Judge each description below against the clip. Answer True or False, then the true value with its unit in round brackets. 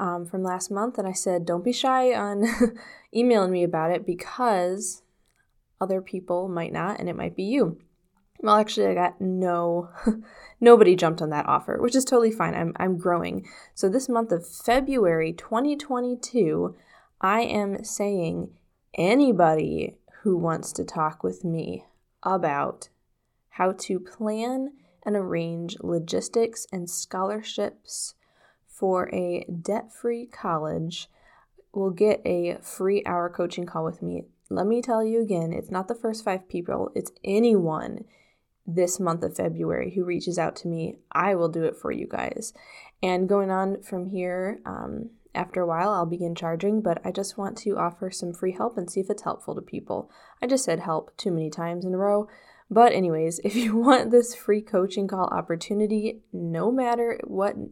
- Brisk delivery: False (165 wpm)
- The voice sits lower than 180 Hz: False (190 Hz)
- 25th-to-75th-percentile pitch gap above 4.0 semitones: True (4.5 semitones)